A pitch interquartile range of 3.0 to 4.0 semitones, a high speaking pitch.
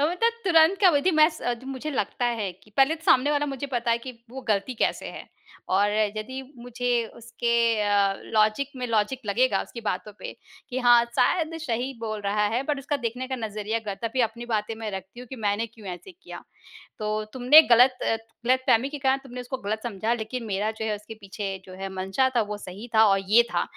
Yes: average, 3.7 semitones; high, 235 Hz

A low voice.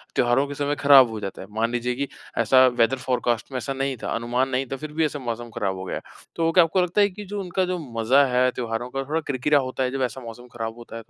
Yes: low, 130 Hz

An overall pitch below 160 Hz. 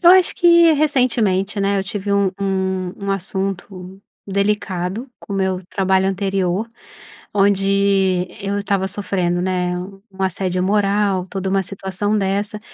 No: high, 195 Hz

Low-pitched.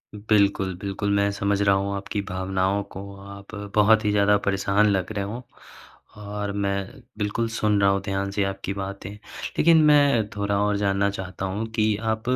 Yes: low, 100 Hz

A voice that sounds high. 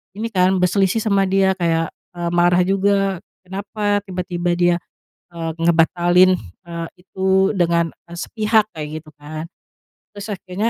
No: medium, 180 Hz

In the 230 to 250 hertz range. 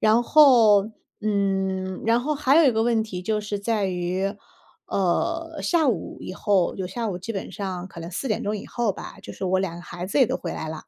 No: high, 205 Hz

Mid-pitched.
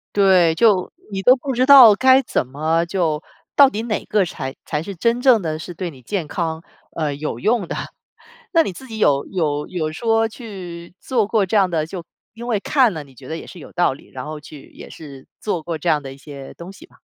Yes: medium, 175 Hz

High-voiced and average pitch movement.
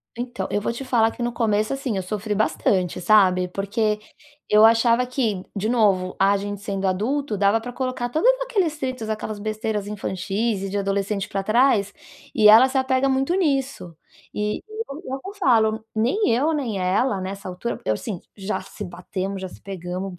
Yes: high, 215 Hz; average, 4.0 semitones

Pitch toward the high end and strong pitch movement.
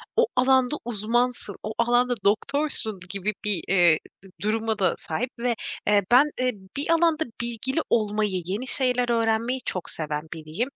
No: high, 235 Hz; average, 3.5 semitones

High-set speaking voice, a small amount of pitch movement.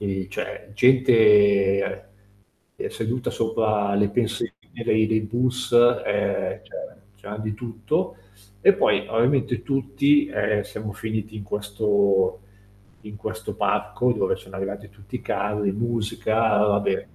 No: low, 105 Hz; narrow, 2.3 semitones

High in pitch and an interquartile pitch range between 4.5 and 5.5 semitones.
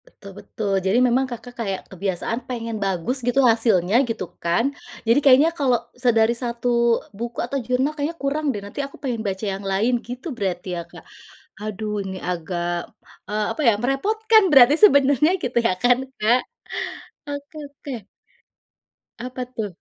Yes: high, 240 Hz; average, 5.1 semitones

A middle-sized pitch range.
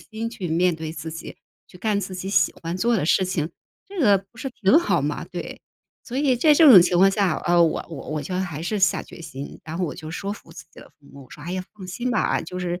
Yes: average, 4.7 semitones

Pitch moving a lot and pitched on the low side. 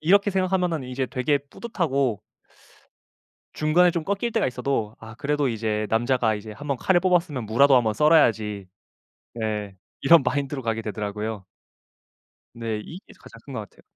Yes: wide, 6.3 semitones; low, 130 Hz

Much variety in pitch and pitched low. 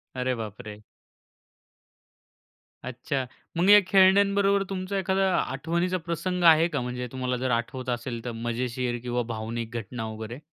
Yes: wide, 7.3 semitones; low, 130 Hz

